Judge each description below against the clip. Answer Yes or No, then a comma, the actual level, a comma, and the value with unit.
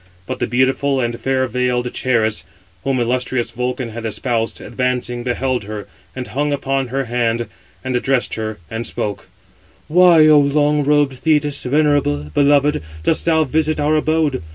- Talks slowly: No, average, 155 wpm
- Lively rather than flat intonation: No, average, 3.4 semitones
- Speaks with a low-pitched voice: Yes, low, 130 Hz